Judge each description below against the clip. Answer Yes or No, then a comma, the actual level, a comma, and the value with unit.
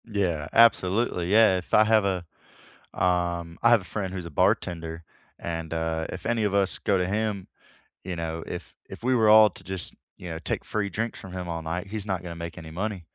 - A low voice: Yes, very low, 90 Hz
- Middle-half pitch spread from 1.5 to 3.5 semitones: No, average, 3.9 semitones